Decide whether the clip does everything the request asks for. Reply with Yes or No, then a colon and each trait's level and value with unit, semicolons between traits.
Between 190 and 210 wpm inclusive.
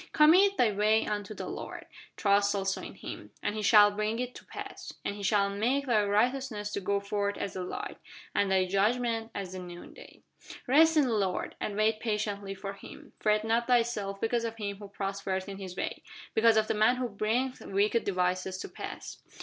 Yes: average, 200 wpm